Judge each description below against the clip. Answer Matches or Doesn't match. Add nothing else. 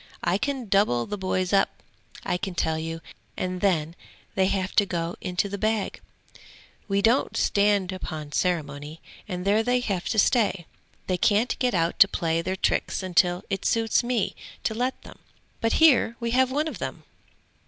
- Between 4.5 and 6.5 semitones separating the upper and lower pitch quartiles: Doesn't match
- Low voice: Doesn't match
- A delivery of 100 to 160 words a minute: Doesn't match